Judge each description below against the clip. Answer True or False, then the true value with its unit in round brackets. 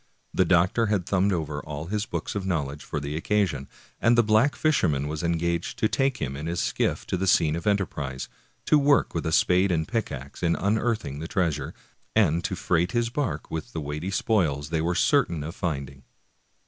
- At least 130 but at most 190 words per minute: False (200 wpm)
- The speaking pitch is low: True (85 Hz)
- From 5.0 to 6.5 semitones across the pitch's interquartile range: True (5.4 semitones)